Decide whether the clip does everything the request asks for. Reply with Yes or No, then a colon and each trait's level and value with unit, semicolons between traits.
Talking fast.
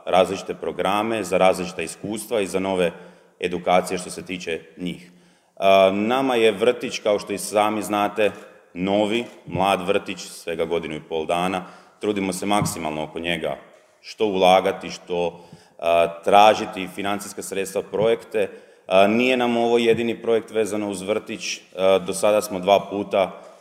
No: average, 135 wpm